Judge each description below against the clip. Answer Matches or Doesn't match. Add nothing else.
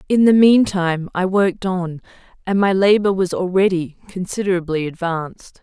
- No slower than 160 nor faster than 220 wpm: Doesn't match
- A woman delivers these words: Matches